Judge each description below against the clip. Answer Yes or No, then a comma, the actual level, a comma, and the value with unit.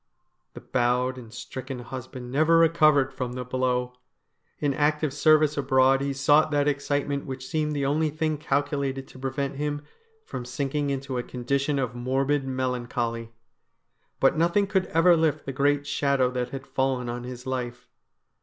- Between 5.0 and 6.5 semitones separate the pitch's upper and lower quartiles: No, narrow, 2.5 semitones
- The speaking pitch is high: No, low, 135 Hz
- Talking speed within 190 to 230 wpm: No, average, 165 wpm